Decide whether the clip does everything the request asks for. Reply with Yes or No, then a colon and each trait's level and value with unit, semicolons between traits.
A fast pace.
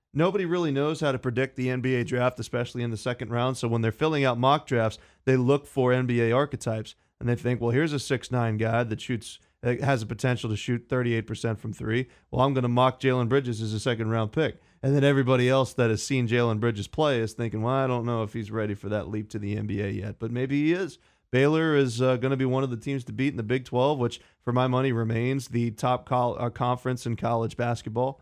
Yes: fast, 245 wpm